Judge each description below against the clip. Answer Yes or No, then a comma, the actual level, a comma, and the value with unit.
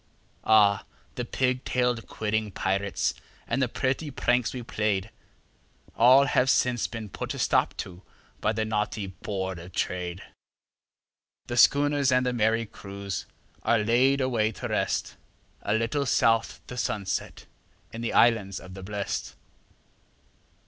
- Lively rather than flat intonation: No, average, 3.8 semitones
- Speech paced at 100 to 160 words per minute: Yes, average, 140 wpm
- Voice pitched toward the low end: Yes, low, 110 Hz